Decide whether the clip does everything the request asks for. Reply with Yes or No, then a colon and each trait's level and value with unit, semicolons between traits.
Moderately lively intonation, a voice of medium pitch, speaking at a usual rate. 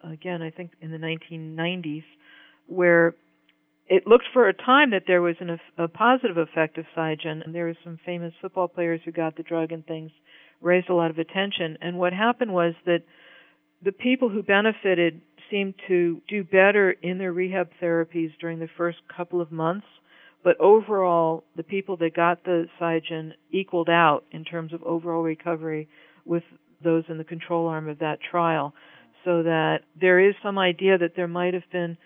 No: narrow, 1.9 semitones; medium, 170 Hz; average, 185 wpm